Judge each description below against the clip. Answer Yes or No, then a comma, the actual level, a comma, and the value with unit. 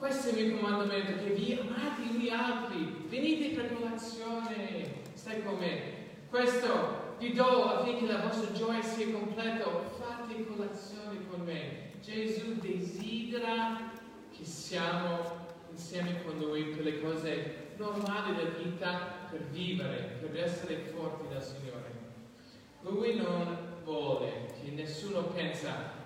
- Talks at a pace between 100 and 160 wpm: Yes, average, 125 wpm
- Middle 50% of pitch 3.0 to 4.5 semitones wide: No, wide, 5.4 semitones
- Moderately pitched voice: No, high, 195 Hz